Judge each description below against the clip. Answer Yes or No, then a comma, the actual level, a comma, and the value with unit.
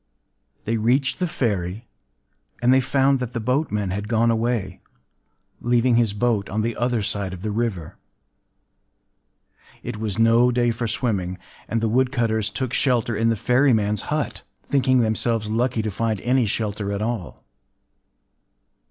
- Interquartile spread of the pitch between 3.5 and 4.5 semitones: No, average, 2.7 semitones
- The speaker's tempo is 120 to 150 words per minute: Yes, average, 145 wpm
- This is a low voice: Yes, low, 115 Hz